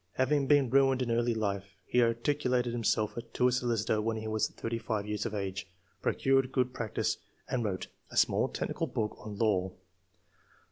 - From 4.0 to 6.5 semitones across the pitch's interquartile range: No, average, 3.0 semitones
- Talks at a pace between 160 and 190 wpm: Yes, average, 175 wpm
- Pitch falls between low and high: No, low, 115 Hz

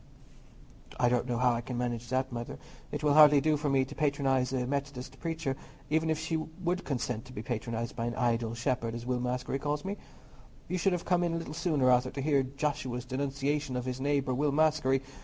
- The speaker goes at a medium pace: No, fast, 215 wpm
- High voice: No, low, 135 Hz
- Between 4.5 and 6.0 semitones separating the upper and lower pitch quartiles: No, average, 3.3 semitones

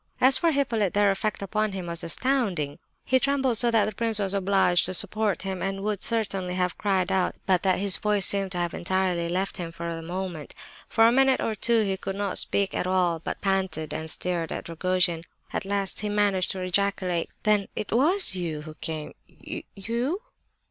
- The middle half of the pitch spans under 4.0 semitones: Yes, average, 2.9 semitones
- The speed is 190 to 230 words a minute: Yes, average, 195 wpm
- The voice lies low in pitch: No, high, 195 Hz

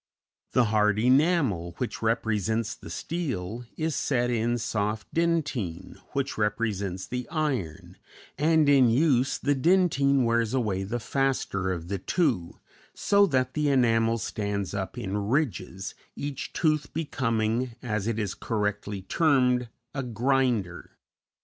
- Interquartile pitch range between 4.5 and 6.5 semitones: Yes, average, 4.9 semitones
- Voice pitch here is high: No, low, 115 Hz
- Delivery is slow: Yes, slow, 130 wpm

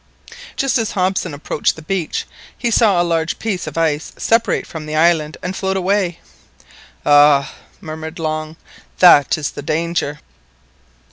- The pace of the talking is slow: No, average, 145 wpm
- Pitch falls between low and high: Yes, medium, 165 Hz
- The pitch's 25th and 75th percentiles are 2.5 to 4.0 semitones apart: Yes, average, 3.5 semitones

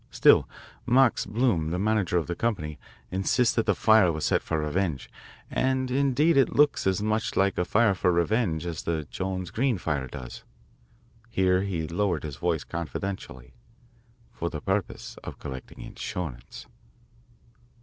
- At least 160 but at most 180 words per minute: No, average, 150 wpm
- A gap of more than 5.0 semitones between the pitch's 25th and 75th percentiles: Yes, wide, 5.4 semitones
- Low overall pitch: Yes, very low, 95 Hz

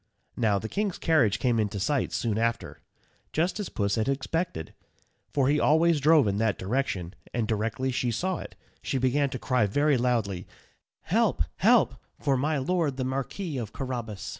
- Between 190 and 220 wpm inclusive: No, average, 170 wpm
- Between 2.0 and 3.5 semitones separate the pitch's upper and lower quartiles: No, average, 4.9 semitones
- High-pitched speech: No, low, 130 Hz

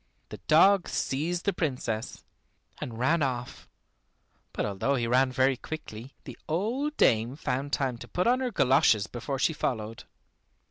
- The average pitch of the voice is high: No, low, 135 Hz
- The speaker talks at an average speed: Yes, average, 150 wpm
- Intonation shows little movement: No, average, 5.3 semitones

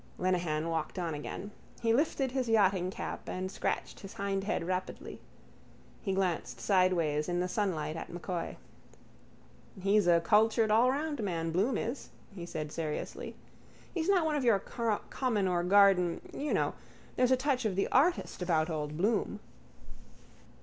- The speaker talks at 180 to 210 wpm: No, average, 145 wpm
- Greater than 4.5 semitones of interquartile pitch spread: Yes, average, 5.0 semitones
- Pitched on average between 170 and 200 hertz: Yes, high, 190 Hz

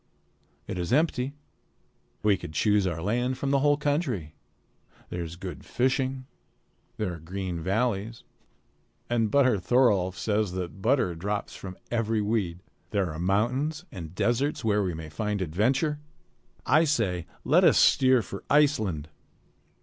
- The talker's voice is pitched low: Yes, low, 105 Hz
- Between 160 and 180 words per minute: No, average, 140 wpm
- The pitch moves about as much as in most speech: No, wide, 6.0 semitones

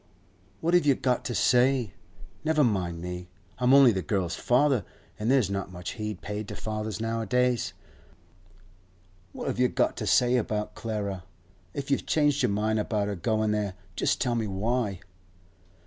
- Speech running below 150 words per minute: No, average, 165 wpm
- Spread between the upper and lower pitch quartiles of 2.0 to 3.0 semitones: No, average, 3.9 semitones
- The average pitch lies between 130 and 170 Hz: No, low, 110 Hz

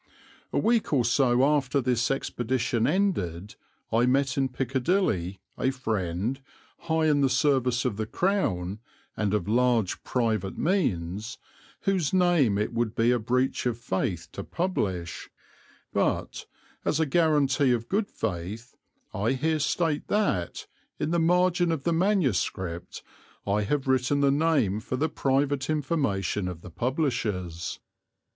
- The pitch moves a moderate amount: No, wide, 6.3 semitones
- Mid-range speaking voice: No, low, 130 Hz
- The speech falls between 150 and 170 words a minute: No, average, 140 wpm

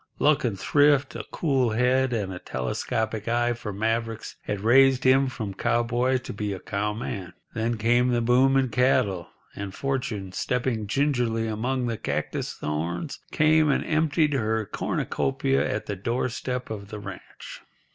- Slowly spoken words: No, average, 155 wpm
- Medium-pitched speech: No, low, 120 Hz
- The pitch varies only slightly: No, average, 3.7 semitones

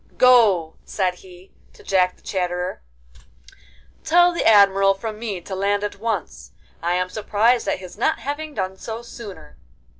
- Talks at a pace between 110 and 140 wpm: No, average, 155 wpm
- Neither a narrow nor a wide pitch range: Yes, average, 3.9 semitones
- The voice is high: Yes, high, 195 Hz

